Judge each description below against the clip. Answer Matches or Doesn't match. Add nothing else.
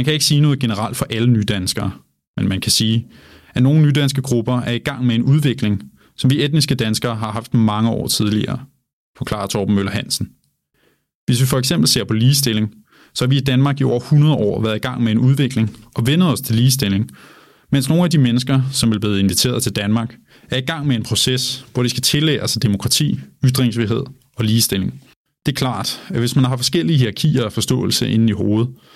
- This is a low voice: Matches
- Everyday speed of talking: Matches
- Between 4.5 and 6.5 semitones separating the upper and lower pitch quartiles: Doesn't match